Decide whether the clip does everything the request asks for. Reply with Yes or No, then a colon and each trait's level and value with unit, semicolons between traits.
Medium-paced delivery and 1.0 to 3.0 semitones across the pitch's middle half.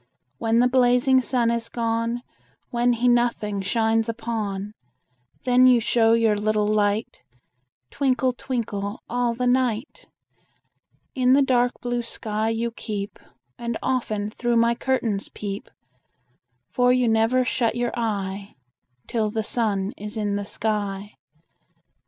No: slow, 130 wpm; narrow, 2.6 semitones